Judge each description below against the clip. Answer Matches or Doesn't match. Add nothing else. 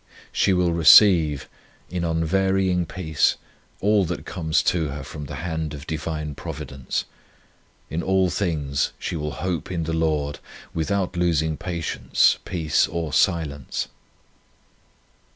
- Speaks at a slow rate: Matches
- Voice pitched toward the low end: Matches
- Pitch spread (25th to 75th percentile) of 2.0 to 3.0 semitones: Matches